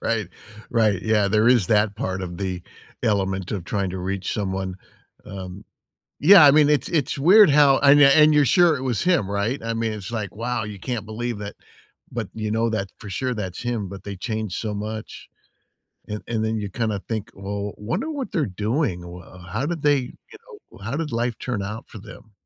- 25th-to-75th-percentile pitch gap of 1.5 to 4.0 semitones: No, average, 4.4 semitones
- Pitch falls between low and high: No, low, 110 Hz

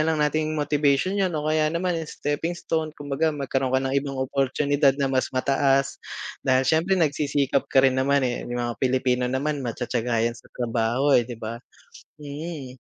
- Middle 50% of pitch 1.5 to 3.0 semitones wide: Yes, average, 2.7 semitones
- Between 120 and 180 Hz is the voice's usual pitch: Yes, medium, 140 Hz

